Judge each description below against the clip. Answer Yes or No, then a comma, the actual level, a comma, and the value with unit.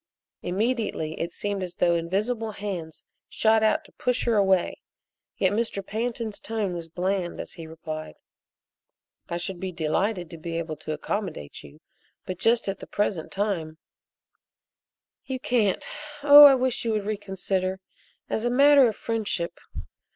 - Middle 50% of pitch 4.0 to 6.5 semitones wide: Yes, average, 4.6 semitones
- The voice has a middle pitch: No, high, 195 Hz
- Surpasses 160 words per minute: No, average, 155 wpm